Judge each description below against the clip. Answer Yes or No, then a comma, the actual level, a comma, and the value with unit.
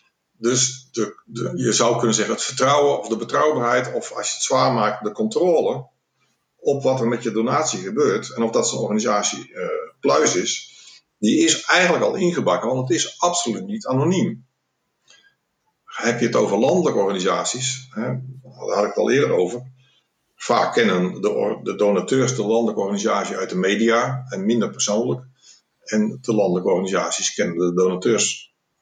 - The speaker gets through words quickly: No, average, 170 wpm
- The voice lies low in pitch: Yes, low, 120 Hz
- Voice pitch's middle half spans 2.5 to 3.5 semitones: Yes, average, 3.0 semitones